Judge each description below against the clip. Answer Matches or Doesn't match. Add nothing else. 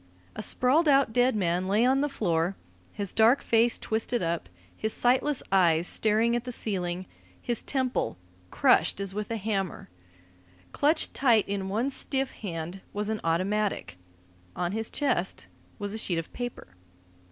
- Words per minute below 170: Matches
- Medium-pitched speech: Doesn't match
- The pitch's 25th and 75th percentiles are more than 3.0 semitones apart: Matches